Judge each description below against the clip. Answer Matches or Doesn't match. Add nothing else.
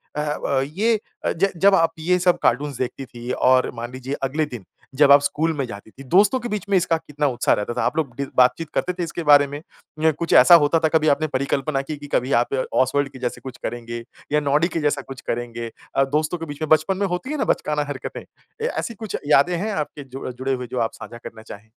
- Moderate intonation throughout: Matches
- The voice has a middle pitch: Matches